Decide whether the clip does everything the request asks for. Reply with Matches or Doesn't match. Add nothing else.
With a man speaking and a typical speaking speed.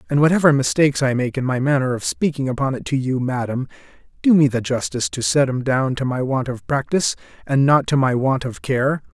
Doesn't match